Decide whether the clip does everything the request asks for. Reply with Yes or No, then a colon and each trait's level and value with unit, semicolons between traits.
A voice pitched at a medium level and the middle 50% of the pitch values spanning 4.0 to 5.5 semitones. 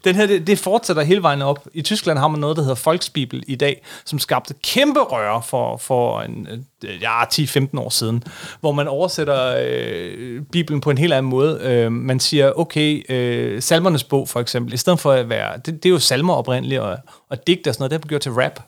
Yes: medium, 145 Hz; average, 4.6 semitones